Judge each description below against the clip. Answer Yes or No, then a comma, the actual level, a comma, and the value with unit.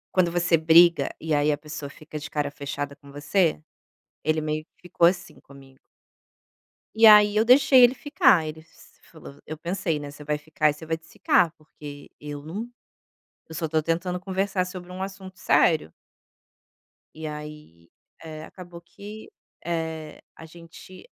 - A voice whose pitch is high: No, medium, 160 Hz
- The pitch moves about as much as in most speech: Yes, average, 3.3 semitones